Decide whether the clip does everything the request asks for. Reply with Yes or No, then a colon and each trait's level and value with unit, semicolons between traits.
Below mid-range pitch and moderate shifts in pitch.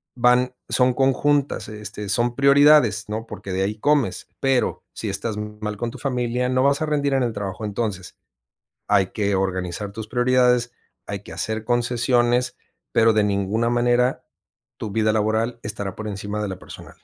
Yes: low, 115 Hz; average, 3.1 semitones